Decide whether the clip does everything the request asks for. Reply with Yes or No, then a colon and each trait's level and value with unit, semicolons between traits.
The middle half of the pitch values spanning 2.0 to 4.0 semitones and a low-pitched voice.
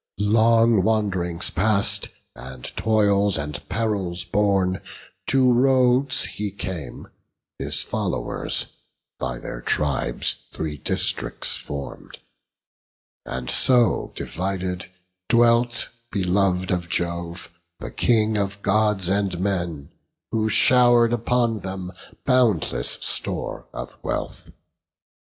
No: average, 4.4 semitones; low, 100 Hz